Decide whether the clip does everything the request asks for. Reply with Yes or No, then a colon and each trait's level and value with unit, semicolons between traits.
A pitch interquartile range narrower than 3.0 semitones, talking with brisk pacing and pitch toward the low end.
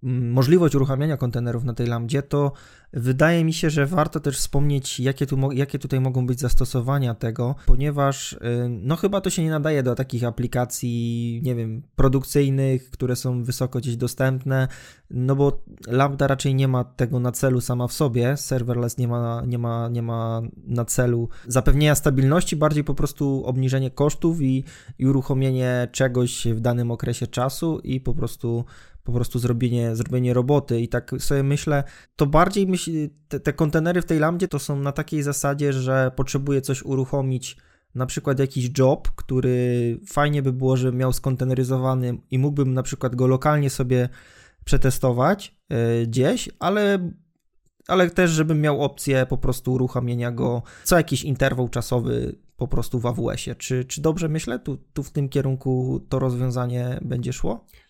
Yes: narrow, 2.5 semitones; fast, 165 wpm; low, 130 Hz